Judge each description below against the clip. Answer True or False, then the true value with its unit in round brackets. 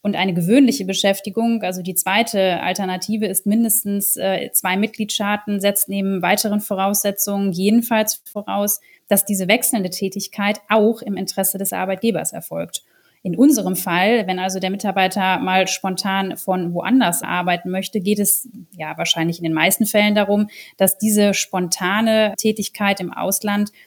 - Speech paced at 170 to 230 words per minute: False (140 wpm)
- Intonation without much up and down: True (2.2 semitones)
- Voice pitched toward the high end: True (200 Hz)